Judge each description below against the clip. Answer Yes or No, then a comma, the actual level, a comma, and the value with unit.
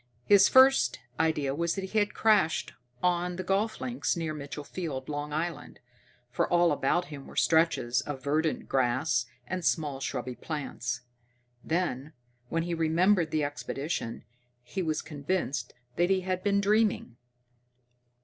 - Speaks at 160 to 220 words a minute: No, average, 145 wpm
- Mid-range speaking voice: Yes, medium, 160 Hz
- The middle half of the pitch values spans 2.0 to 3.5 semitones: No, average, 4.5 semitones